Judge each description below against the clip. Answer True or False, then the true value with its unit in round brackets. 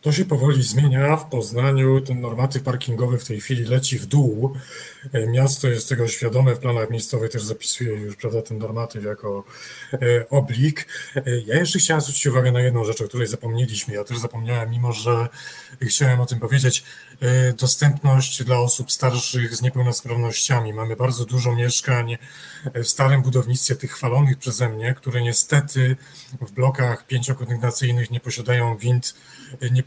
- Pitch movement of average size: False (2.0 semitones)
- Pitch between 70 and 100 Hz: False (125 Hz)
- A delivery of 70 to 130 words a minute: False (155 wpm)